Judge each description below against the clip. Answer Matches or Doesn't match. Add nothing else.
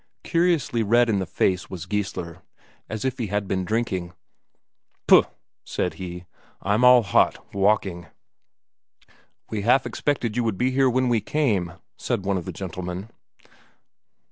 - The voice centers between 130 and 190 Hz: Doesn't match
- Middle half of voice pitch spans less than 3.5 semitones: Doesn't match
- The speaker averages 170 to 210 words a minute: Doesn't match